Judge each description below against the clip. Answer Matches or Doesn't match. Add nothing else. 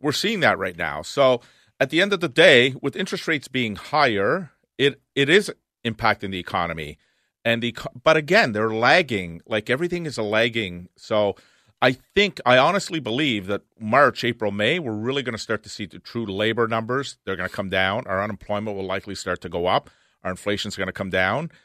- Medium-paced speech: Doesn't match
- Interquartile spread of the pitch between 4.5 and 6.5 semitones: Matches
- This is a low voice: Matches